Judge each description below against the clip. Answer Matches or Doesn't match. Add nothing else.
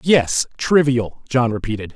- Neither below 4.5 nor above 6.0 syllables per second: Doesn't match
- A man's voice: Matches